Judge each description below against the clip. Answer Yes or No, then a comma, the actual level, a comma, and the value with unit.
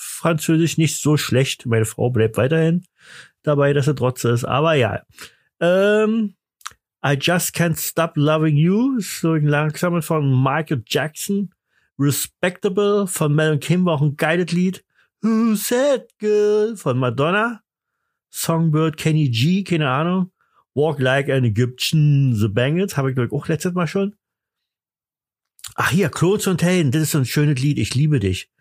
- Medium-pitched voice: Yes, medium, 160 Hz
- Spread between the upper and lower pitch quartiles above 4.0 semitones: Yes, average, 4.6 semitones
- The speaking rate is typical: Yes, average, 150 wpm